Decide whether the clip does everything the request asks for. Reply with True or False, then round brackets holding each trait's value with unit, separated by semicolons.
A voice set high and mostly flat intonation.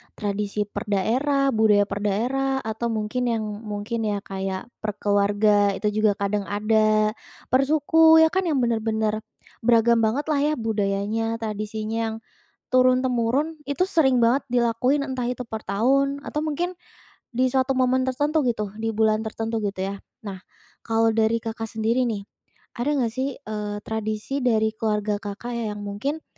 False (225 Hz; 3.5 semitones)